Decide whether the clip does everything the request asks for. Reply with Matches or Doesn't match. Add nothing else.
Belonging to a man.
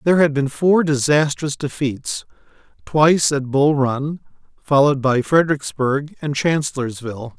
Matches